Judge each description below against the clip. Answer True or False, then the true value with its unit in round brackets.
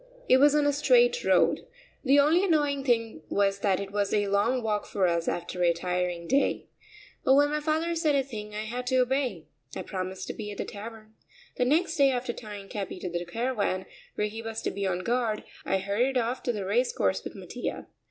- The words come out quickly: True (220 wpm)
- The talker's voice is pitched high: True (225 Hz)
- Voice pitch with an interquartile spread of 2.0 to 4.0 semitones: False (5.5 semitones)